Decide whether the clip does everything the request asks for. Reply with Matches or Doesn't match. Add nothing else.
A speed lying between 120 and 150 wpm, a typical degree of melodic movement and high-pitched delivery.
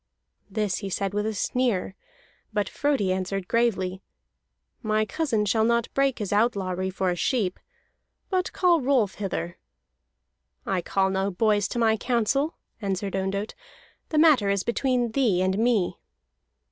Matches